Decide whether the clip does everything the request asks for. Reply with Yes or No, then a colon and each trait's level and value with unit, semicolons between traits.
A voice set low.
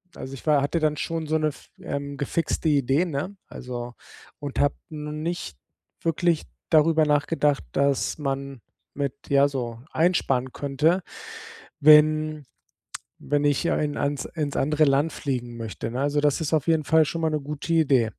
No: medium, 145 Hz